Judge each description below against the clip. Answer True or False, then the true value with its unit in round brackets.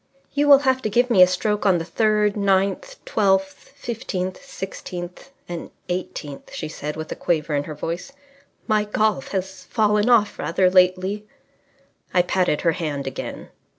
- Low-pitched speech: False (190 Hz)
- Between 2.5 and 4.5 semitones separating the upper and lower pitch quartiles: True (3.4 semitones)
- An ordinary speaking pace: True (160 wpm)